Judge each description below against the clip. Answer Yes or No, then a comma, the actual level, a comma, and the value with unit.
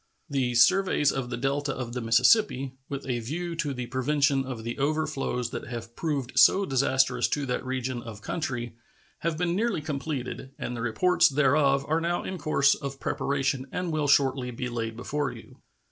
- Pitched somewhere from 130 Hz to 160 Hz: Yes, low, 135 Hz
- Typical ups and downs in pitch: Yes, average, 3.4 semitones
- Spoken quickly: No, average, 180 wpm